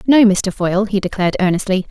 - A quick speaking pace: No, average, 190 wpm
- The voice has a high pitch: Yes, high, 200 Hz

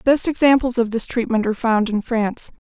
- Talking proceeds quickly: Yes, fast, 225 wpm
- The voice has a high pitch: Yes, high, 235 Hz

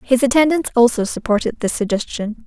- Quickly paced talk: No, average, 145 wpm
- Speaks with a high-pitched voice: Yes, high, 240 Hz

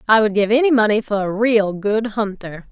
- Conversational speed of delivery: No, fast, 220 wpm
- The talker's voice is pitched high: Yes, high, 215 Hz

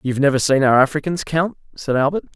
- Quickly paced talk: Yes, fast, 230 wpm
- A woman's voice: No, male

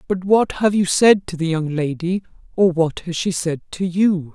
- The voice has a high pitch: No, medium, 180 Hz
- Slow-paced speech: No, fast, 205 wpm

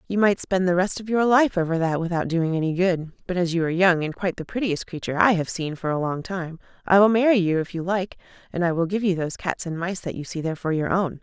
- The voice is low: No, medium, 175 Hz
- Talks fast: Yes, fast, 290 wpm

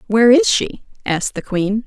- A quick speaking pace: No, average, 195 wpm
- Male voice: No, female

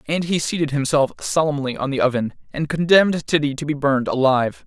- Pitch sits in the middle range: Yes, medium, 145 Hz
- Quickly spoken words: No, average, 195 wpm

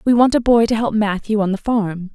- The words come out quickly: Yes, fast, 280 wpm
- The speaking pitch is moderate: No, high, 215 Hz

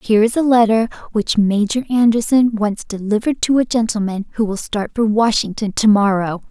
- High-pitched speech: Yes, high, 220 Hz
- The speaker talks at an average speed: Yes, average, 175 wpm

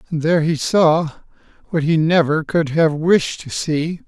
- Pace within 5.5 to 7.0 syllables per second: No, 3.9 syllables/s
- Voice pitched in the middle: Yes, medium, 160 Hz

